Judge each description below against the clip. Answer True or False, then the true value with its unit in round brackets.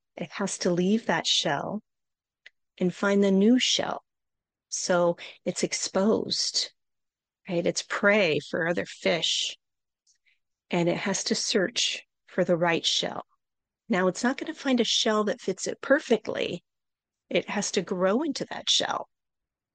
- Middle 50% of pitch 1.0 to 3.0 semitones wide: False (4.8 semitones)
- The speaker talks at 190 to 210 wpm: False (145 wpm)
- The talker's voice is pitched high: True (200 Hz)